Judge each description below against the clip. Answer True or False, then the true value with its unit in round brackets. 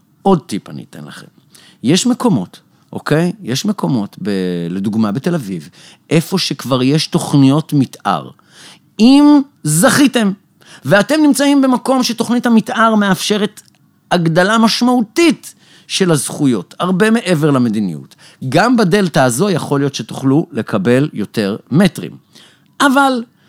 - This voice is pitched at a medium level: True (180 Hz)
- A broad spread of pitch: True (8.1 semitones)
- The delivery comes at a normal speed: True (110 wpm)